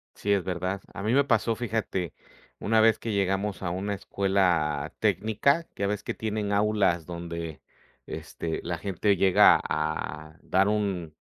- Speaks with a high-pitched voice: No, low, 100 Hz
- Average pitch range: Yes, average, 3.4 semitones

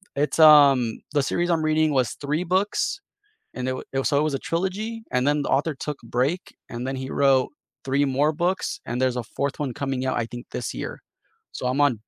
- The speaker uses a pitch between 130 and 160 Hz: Yes, medium, 140 Hz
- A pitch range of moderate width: Yes, average, 3.3 semitones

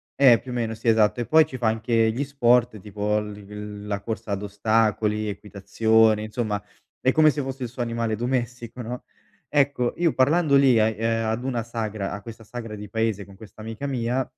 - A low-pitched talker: Yes, low, 115 Hz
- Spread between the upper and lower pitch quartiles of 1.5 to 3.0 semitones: Yes, average, 2.7 semitones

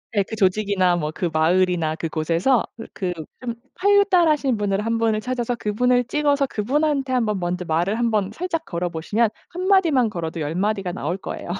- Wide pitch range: Yes, wide, 6.3 semitones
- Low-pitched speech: No, high, 210 Hz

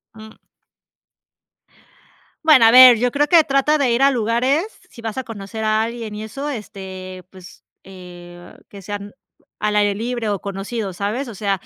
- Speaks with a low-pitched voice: No, high, 220 Hz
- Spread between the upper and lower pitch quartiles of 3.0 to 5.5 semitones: Yes, average, 3.9 semitones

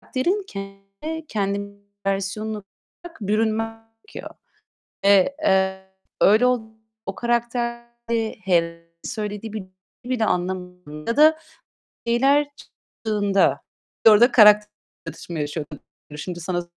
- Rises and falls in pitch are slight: No, average, 3.8 semitones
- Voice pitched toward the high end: Yes, high, 210 Hz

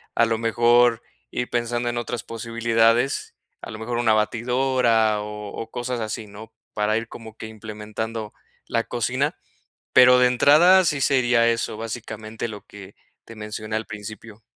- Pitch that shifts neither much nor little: No, narrow, 1.9 semitones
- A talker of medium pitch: No, low, 115 Hz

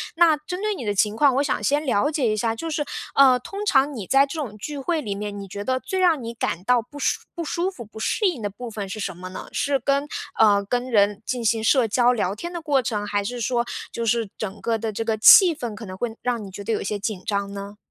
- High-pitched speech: Yes, high, 235 Hz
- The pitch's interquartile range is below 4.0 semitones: No, average, 5.3 semitones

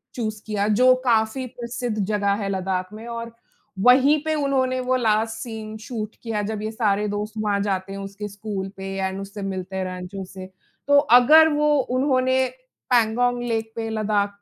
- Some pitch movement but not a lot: Yes, average, 3.5 semitones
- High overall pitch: Yes, high, 220 Hz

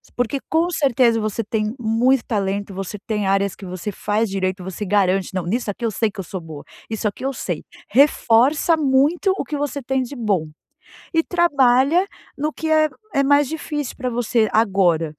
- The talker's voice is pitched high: Yes, high, 230 Hz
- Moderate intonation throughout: No, wide, 5.9 semitones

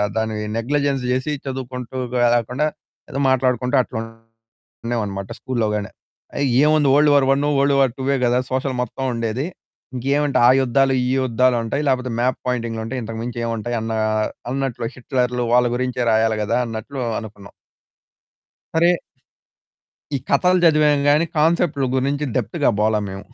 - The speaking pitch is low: Yes, low, 125 Hz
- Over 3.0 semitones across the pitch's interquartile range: Yes, average, 3.4 semitones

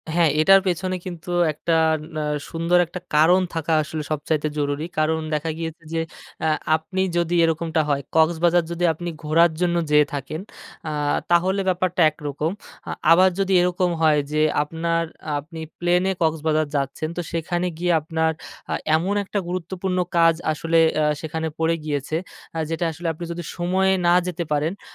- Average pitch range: No, narrow, 2.0 semitones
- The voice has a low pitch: No, medium, 165 Hz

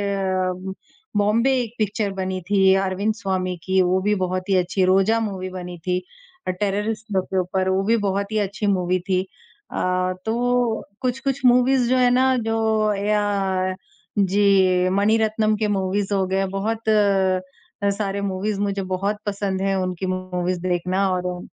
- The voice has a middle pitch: No, high, 195 Hz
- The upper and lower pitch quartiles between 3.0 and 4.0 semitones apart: No, narrow, 2.4 semitones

